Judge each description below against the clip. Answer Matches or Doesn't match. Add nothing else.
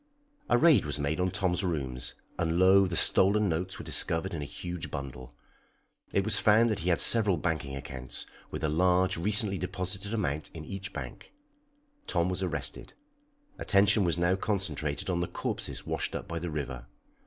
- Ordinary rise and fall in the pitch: Matches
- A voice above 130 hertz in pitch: Doesn't match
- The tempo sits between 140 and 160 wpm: Doesn't match